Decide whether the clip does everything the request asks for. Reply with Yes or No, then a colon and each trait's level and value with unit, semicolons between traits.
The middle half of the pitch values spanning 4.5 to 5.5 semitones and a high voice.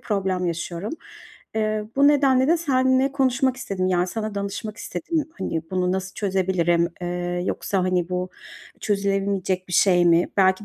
Yes: average, 4.8 semitones; high, 195 Hz